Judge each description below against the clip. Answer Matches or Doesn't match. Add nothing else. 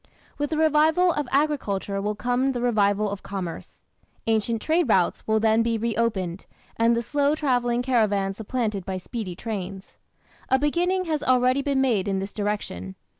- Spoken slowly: Doesn't match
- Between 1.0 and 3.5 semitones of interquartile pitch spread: Doesn't match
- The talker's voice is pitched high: Matches